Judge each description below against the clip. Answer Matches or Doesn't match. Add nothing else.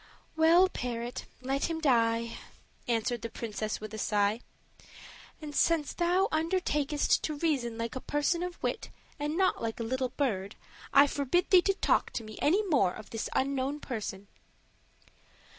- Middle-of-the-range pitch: Doesn't match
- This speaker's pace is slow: Doesn't match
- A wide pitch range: Matches